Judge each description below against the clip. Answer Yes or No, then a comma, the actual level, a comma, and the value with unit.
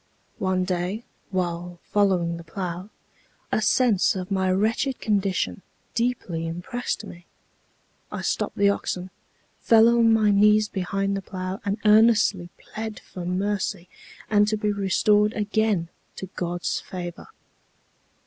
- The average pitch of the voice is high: Yes, high, 195 Hz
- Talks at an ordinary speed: No, slow, 130 wpm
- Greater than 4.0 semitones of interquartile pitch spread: No, average, 2.7 semitones